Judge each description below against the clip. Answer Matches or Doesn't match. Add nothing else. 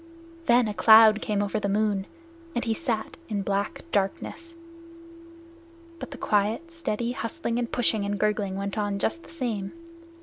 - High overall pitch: Matches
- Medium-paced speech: Matches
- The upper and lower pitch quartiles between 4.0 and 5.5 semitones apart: Doesn't match